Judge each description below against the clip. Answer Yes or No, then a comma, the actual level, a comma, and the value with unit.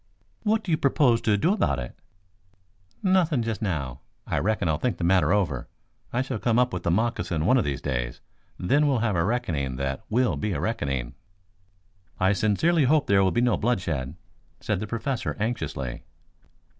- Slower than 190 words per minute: Yes, average, 180 wpm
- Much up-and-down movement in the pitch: Yes, wide, 7.6 semitones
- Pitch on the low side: Yes, low, 105 Hz